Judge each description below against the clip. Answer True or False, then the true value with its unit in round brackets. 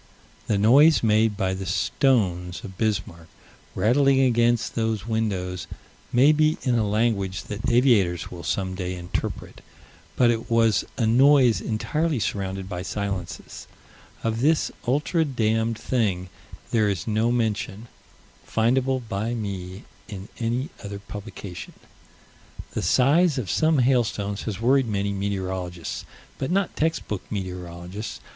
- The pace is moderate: False (130 wpm)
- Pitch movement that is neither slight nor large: True (4.2 semitones)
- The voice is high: False (110 Hz)